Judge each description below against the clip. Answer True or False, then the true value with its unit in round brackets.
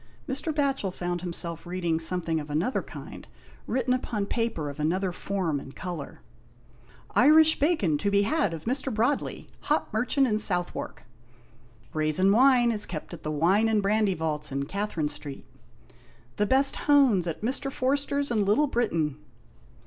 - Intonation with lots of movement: True (7.6 semitones)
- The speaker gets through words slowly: False (165 wpm)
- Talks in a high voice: True (200 Hz)